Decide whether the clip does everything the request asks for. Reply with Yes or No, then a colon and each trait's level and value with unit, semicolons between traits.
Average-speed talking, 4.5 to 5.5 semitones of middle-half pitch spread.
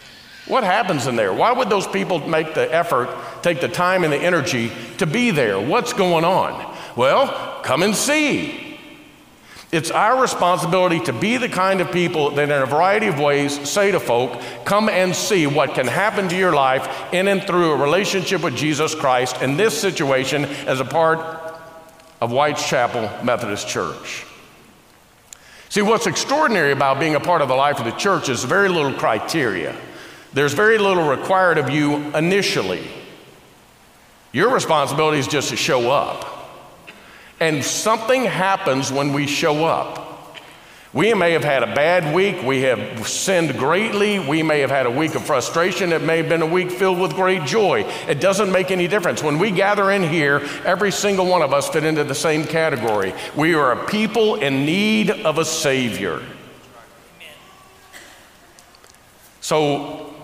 Yes: average, 170 wpm; average, 4.9 semitones